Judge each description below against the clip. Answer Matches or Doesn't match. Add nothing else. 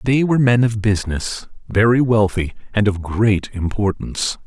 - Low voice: Matches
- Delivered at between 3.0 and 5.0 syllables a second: Matches